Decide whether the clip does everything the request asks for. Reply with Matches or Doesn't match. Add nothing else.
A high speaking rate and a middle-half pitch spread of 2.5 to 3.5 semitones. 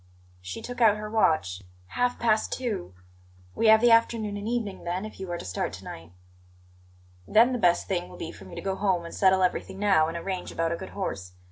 Doesn't match